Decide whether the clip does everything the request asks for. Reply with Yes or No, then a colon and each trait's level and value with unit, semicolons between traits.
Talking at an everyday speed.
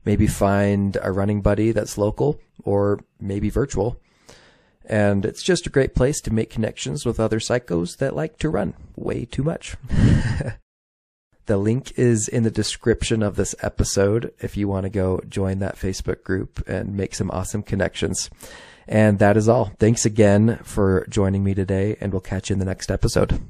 Yes: average, 180 wpm